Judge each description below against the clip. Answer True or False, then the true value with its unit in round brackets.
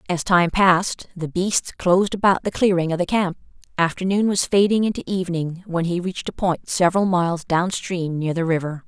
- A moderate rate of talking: True (190 wpm)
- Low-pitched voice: False (180 Hz)